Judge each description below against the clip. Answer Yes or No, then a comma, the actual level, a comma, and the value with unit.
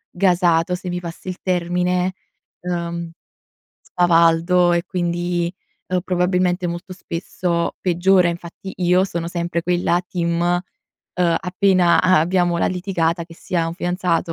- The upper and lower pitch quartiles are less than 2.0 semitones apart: Yes, narrow, 1.0 semitones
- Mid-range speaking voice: Yes, medium, 175 Hz